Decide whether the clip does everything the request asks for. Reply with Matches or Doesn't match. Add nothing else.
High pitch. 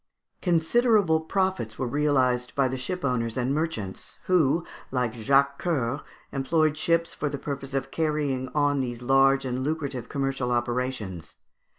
Doesn't match